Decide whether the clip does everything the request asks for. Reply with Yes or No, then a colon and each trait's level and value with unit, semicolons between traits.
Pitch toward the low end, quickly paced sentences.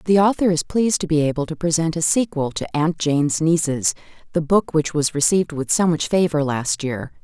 No: medium, 160 Hz; fast, 215 wpm